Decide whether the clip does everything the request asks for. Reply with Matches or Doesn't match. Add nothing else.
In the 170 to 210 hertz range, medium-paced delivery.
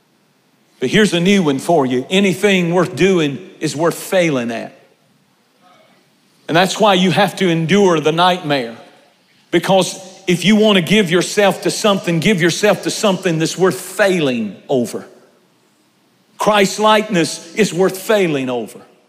Matches